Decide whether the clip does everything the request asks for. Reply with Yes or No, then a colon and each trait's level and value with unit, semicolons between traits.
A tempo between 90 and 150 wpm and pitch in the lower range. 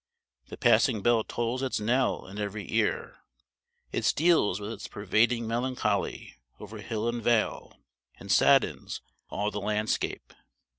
Yes: slow, 135 wpm; low, 110 Hz